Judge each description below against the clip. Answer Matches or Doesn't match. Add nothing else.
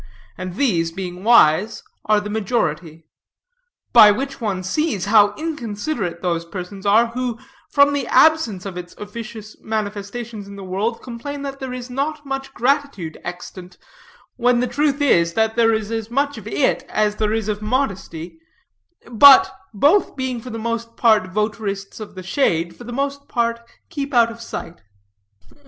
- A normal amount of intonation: Matches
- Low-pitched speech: Doesn't match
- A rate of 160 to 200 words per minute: Matches